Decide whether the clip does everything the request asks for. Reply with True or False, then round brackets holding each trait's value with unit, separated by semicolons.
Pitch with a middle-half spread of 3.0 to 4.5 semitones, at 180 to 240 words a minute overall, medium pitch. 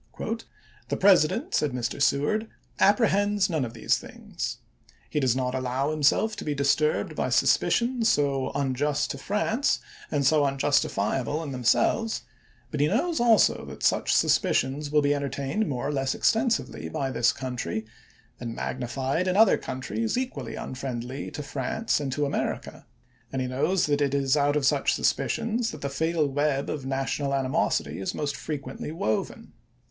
False (3.7 semitones; 165 wpm; 145 Hz)